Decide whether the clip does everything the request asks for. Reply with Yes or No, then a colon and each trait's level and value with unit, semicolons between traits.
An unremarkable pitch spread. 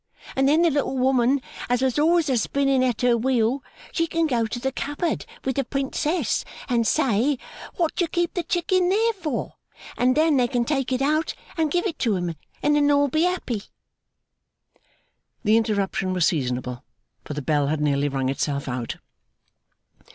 No: wide, 6.0 semitones